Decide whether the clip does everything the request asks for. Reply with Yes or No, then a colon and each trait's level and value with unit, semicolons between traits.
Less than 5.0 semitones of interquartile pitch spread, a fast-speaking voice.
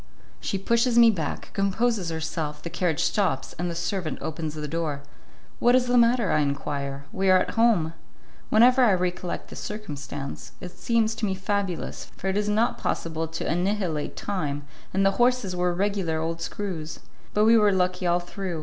No: average, 4.5 semitones; average, 180 wpm